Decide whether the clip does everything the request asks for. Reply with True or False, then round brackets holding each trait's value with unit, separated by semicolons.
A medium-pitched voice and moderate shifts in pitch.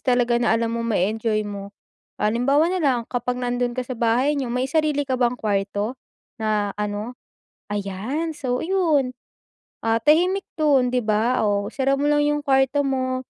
False (250 Hz; 3.9 semitones)